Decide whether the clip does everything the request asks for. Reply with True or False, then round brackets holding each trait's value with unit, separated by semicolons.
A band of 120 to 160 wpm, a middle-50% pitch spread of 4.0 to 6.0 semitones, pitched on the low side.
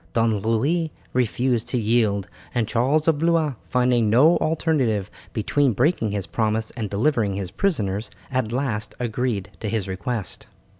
True (145 wpm; 4.4 semitones; 115 Hz)